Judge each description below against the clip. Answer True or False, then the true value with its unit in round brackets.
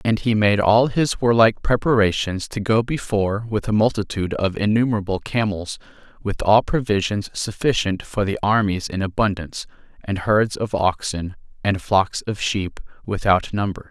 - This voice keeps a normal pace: True (150 wpm)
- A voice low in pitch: True (105 Hz)